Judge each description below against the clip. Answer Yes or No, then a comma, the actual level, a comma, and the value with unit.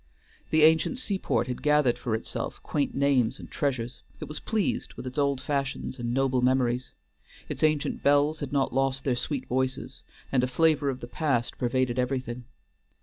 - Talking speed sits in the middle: Yes, average, 175 wpm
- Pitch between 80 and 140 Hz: Yes, low, 135 Hz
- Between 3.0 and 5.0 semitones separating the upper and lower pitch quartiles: No, narrow, 2.6 semitones